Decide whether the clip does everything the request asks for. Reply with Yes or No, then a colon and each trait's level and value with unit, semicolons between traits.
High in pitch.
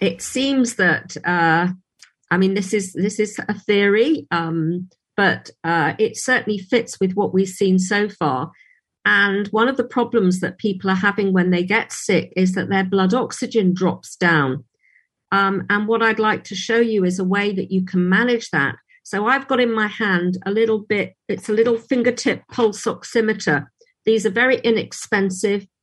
Yes: high, 205 Hz